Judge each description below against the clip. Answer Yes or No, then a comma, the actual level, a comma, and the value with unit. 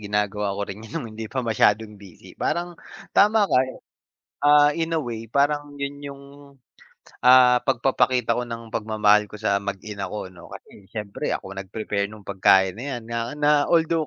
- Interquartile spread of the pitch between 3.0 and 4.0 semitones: No, average, 5.3 semitones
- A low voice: Yes, low, 115 Hz